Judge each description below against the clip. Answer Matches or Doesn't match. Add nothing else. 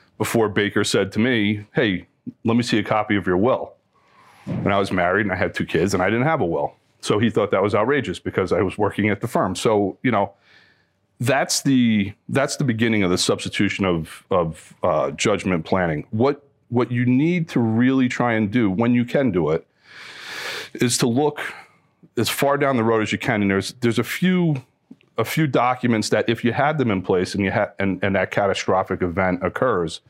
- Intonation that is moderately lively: Matches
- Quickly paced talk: Matches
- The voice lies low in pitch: Matches